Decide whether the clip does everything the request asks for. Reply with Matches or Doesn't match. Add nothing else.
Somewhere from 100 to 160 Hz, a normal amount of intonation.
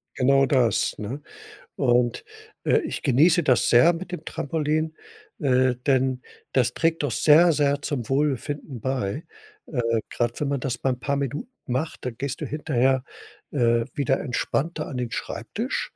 Matches